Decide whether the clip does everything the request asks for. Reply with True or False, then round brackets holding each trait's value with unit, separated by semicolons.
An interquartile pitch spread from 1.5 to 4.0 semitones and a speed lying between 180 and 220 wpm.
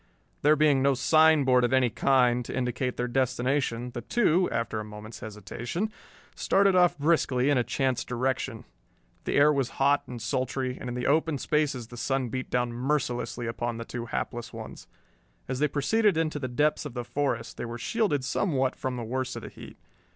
True (3.2 semitones; 190 wpm)